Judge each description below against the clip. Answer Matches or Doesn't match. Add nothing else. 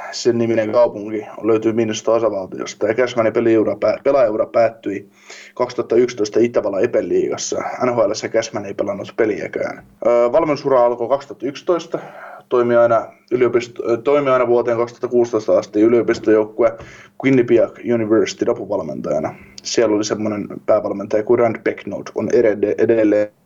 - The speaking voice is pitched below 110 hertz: Doesn't match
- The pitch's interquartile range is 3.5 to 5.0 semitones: Matches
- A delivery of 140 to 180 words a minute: Doesn't match